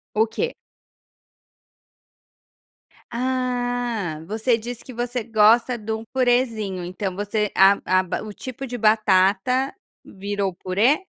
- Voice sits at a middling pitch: No, high, 220 Hz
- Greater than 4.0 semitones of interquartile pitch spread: No, average, 3.6 semitones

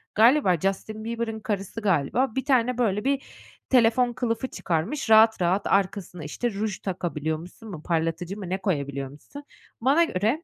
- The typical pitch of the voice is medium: No, high, 210 Hz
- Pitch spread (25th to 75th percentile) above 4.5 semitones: Yes, average, 5.1 semitones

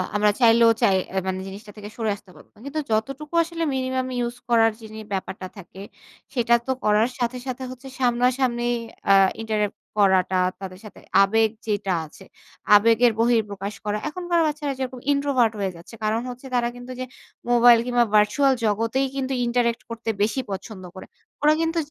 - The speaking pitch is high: Yes, high, 230 Hz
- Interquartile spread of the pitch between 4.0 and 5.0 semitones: No, average, 3.6 semitones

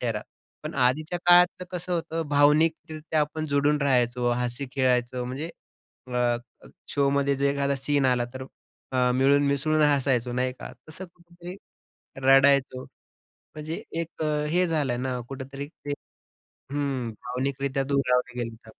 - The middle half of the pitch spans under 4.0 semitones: Yes, average, 3.3 semitones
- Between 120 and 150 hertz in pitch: Yes, medium, 140 Hz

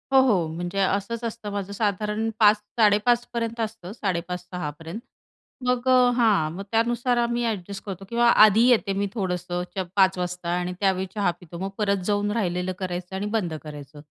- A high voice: Yes, high, 200 Hz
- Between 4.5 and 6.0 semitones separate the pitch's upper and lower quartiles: No, average, 3.9 semitones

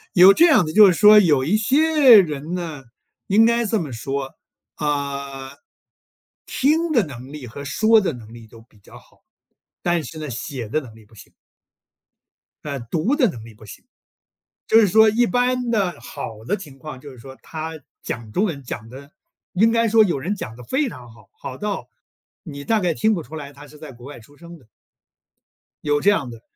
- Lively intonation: Yes, wide, 8.1 semitones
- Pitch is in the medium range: Yes, medium, 155 Hz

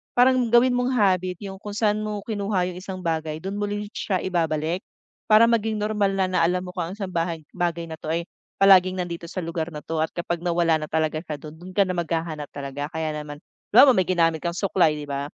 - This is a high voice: No, medium, 180 Hz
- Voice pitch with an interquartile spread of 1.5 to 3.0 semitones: No, average, 3.8 semitones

